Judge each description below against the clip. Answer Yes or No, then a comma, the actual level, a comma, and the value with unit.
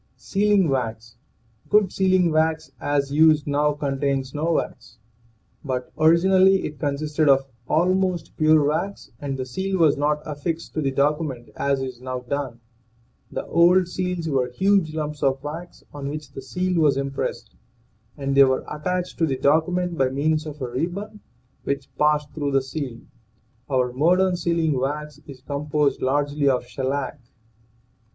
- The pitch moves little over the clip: No, average, 3.5 semitones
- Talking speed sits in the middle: Yes, average, 155 wpm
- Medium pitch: Yes, medium, 150 Hz